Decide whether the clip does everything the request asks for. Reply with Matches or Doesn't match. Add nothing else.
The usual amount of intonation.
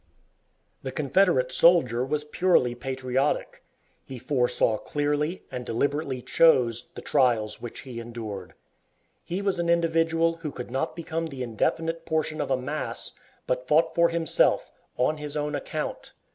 Matches